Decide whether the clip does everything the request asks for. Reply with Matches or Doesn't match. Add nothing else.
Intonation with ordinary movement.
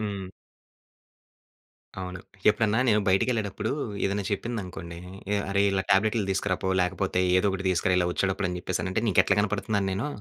Doesn't match